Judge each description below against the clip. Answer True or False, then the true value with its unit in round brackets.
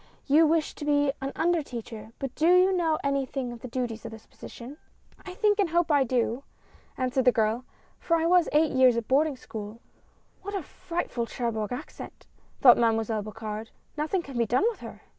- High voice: True (265 Hz)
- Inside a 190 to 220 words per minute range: True (200 wpm)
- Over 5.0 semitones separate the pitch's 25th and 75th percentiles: True (5.6 semitones)